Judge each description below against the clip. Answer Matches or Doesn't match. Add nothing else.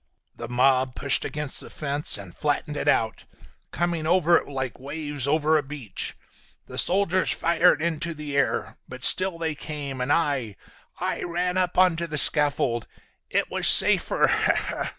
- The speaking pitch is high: Doesn't match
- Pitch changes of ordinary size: Matches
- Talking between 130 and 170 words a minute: Matches